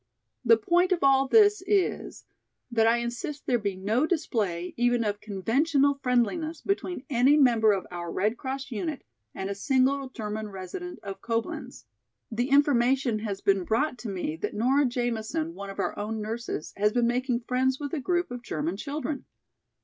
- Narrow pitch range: No, average, 4.8 semitones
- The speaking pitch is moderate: No, high, 245 Hz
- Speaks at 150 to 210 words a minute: Yes, average, 170 wpm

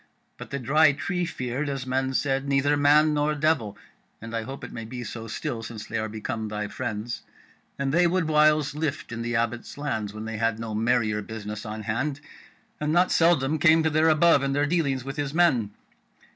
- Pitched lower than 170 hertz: Yes, low, 135 Hz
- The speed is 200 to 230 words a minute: Yes, fast, 205 wpm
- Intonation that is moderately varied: Yes, average, 5.0 semitones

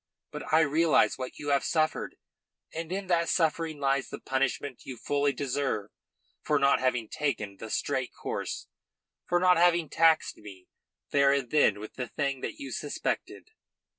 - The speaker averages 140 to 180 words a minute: Yes, average, 165 wpm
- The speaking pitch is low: No, medium, 145 Hz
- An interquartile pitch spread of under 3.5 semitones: No, average, 3.9 semitones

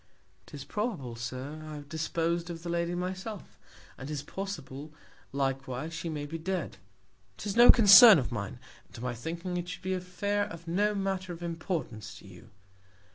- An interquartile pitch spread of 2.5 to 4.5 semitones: No, average, 5.1 semitones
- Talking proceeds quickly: No, average, 180 wpm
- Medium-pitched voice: Yes, medium, 165 Hz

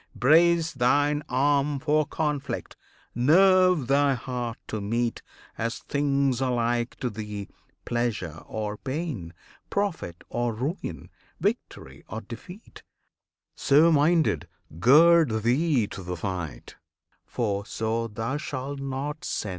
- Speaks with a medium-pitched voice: No, low, 130 Hz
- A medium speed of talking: No, slow, 115 wpm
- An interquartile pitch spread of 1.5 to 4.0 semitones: No, average, 4.7 semitones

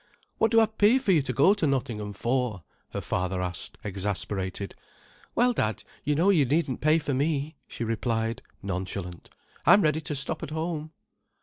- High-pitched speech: No, low, 135 Hz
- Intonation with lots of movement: Yes, wide, 7.6 semitones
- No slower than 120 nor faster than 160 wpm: No, average, 175 wpm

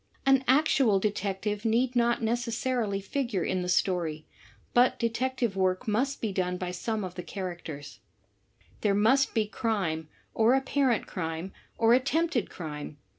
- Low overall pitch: No, high, 215 Hz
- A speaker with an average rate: No, slow, 130 wpm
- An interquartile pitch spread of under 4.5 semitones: No, average, 4.9 semitones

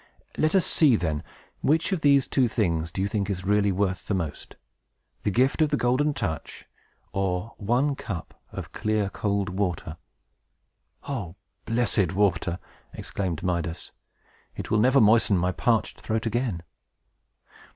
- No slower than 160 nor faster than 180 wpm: No, average, 145 wpm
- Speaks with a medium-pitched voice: No, low, 100 Hz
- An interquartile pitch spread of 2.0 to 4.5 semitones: No, average, 5.1 semitones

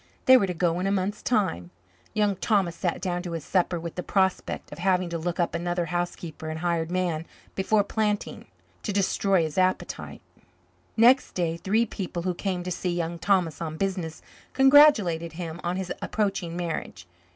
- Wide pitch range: No, narrow, 2.6 semitones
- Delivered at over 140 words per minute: Yes, average, 180 wpm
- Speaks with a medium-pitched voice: Yes, medium, 180 Hz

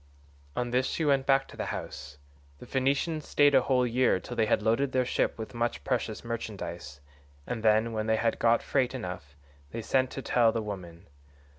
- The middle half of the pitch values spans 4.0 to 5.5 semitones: No, average, 3.2 semitones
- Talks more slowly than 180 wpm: No, average, 195 wpm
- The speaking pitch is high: No, low, 115 Hz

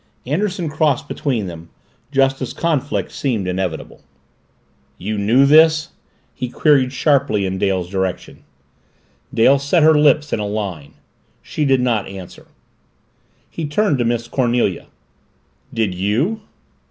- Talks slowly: Yes, slow, 130 wpm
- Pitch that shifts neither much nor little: No, wide, 6.7 semitones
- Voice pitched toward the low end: Yes, low, 125 Hz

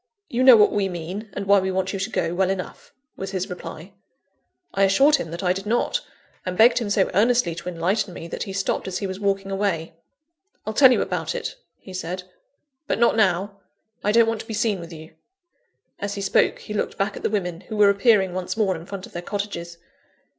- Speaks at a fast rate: Yes, fast, 225 wpm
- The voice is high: Yes, high, 195 Hz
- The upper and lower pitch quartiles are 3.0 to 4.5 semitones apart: No, narrow, 2.6 semitones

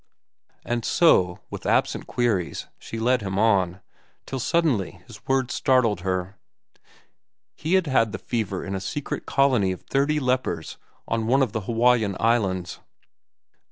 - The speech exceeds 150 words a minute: No, average, 145 wpm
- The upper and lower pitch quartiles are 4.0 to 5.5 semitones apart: Yes, average, 5.2 semitones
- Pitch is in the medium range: No, low, 115 Hz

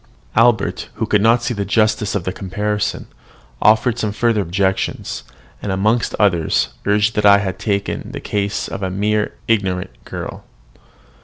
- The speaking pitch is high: No, low, 105 Hz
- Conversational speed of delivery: Yes, average, 160 wpm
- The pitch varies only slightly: Yes, narrow, 1.8 semitones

